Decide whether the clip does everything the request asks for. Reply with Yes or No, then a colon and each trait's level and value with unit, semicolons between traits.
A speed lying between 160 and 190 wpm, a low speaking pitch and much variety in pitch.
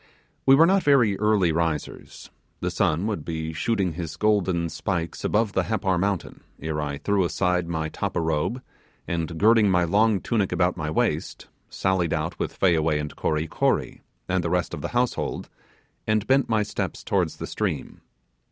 No: average, 170 wpm; very low, 90 Hz; average, 4.7 semitones